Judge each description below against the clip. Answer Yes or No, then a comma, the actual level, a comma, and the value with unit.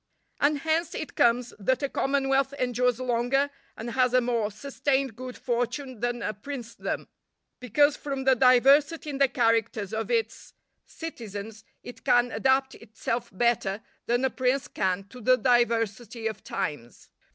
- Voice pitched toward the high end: Yes, very high, 250 Hz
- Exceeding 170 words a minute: No, average, 150 wpm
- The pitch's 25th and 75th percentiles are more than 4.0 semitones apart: No, average, 2.9 semitones